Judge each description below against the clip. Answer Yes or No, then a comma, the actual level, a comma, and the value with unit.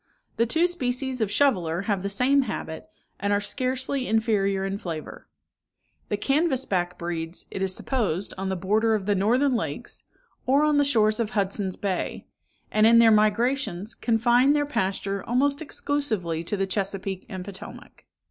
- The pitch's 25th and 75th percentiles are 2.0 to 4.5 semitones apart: No, average, 4.9 semitones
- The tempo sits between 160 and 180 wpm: Yes, average, 165 wpm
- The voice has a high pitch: Yes, high, 215 Hz